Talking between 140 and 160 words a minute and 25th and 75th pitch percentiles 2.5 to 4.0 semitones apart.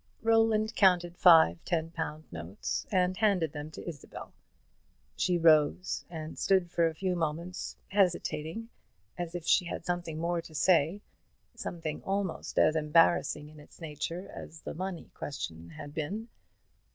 Yes: average, 145 wpm; average, 2.9 semitones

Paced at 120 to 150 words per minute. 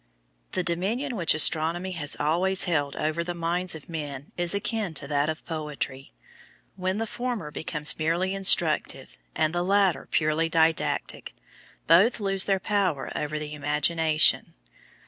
Yes: average, 145 wpm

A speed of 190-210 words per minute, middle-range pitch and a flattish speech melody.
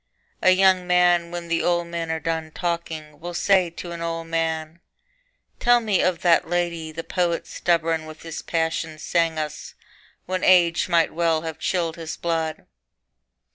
No: average, 165 wpm; medium, 170 Hz; narrow, 1.4 semitones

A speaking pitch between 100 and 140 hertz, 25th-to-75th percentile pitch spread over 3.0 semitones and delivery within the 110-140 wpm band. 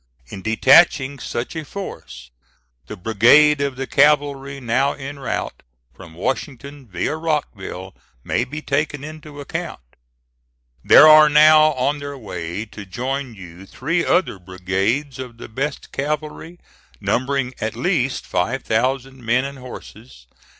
Yes: low, 135 Hz; average, 4.8 semitones; slow, 135 wpm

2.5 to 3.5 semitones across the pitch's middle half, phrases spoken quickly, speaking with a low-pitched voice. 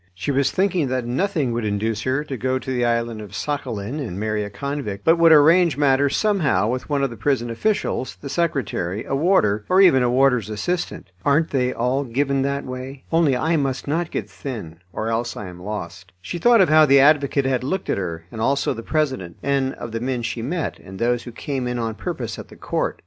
No: average, 4.4 semitones; fast, 225 wpm; low, 130 Hz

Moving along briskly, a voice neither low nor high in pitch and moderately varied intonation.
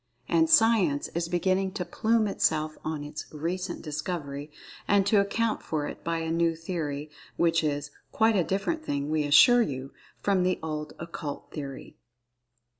No: average, 160 wpm; medium, 165 Hz; average, 4.2 semitones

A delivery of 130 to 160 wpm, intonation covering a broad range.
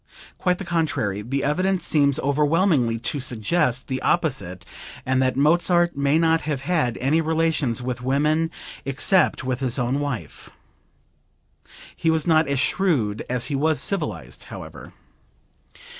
No: average, 140 wpm; average, 4.2 semitones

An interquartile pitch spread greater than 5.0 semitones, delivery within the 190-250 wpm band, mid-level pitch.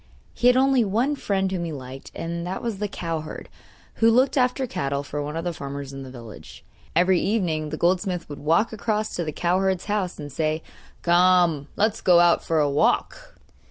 Yes: wide, 5.4 semitones; average, 195 wpm; medium, 175 Hz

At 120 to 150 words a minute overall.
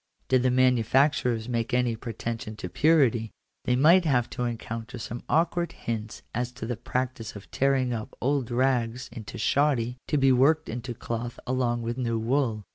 No: average, 170 wpm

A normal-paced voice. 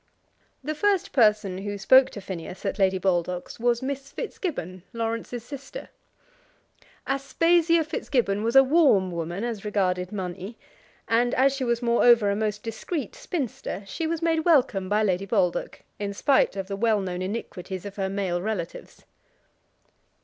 Yes: average, 150 wpm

